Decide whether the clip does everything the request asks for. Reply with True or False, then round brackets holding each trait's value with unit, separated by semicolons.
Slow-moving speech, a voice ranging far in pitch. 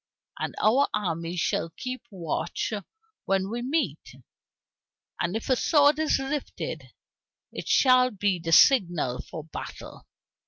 True (125 wpm; 7.6 semitones)